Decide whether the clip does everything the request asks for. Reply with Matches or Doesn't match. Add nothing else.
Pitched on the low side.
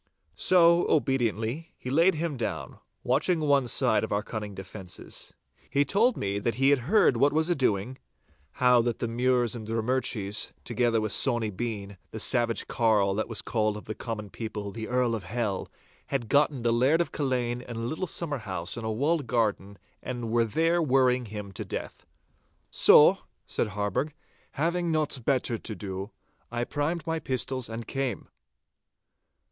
Matches